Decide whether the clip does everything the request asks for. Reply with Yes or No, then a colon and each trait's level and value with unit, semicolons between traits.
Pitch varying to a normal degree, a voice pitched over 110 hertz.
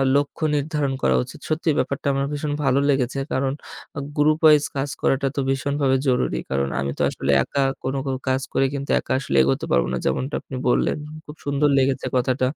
No: narrow, 1.8 semitones; low, 135 Hz